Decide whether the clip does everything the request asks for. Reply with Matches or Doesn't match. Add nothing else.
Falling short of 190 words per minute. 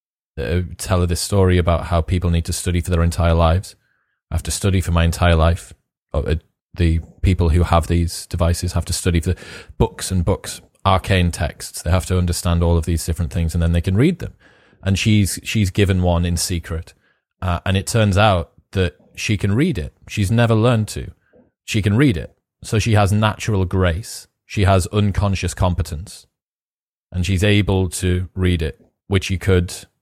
Doesn't match